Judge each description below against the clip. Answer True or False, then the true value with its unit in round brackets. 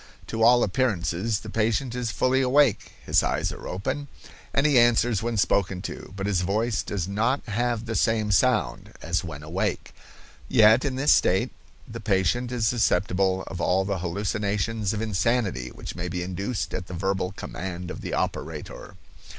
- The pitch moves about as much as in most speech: True (4.2 semitones)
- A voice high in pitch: False (105 Hz)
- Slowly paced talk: False (170 wpm)